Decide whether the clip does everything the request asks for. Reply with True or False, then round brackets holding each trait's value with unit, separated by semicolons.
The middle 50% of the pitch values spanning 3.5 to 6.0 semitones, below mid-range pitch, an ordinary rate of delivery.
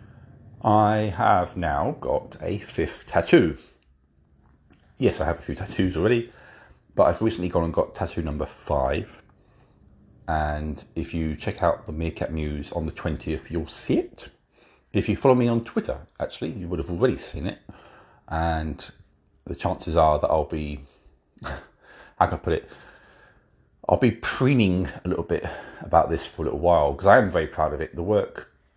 True (5.2 semitones; 80 Hz; 175 wpm)